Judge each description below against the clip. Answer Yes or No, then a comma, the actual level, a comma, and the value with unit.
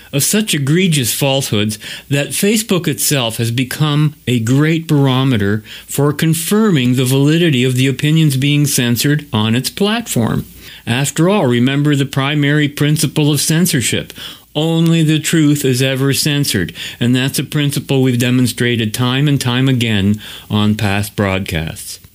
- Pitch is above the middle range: No, medium, 140 Hz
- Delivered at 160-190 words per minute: No, average, 140 wpm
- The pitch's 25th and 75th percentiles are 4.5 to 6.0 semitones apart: No, average, 3.8 semitones